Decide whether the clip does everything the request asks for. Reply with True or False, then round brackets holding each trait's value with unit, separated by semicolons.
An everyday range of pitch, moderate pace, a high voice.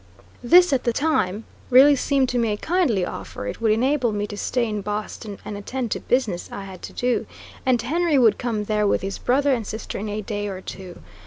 False (4.0 semitones; 225 wpm; 225 Hz)